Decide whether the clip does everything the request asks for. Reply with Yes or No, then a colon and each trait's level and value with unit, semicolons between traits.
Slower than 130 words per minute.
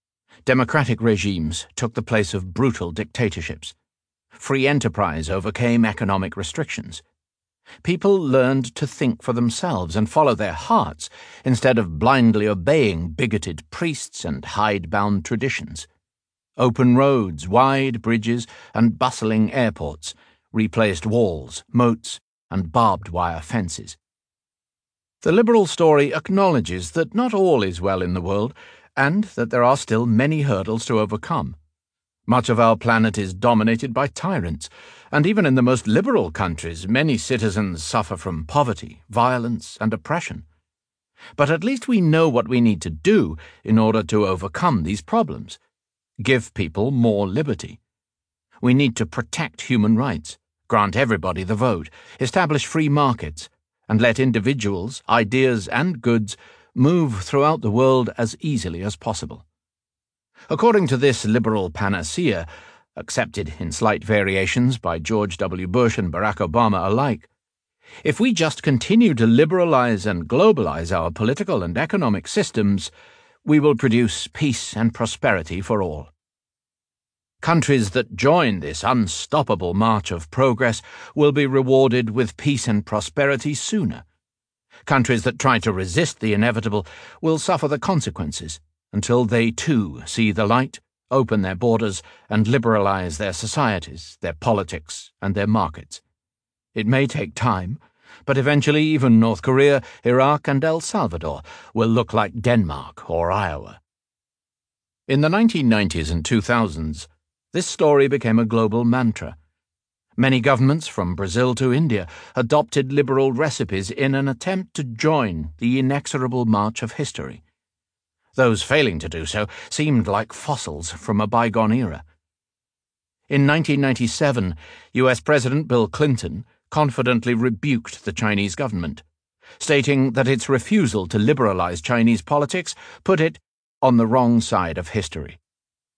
No: fast, 135 wpm